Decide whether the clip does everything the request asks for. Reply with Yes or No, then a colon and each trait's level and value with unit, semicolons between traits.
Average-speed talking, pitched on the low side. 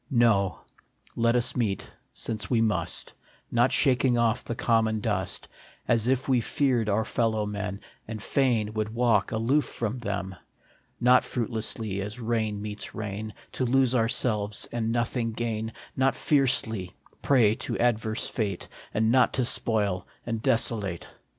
Yes: average, 145 wpm; low, 115 Hz